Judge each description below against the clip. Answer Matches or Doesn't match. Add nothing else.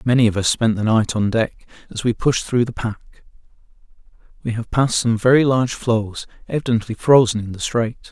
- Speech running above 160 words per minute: Matches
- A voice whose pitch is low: Matches